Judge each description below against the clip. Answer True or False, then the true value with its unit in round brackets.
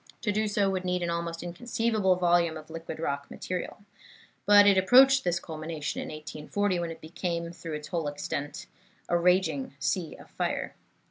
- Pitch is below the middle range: False (175 Hz)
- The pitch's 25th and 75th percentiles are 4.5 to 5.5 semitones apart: False (3.4 semitones)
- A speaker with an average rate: True (175 wpm)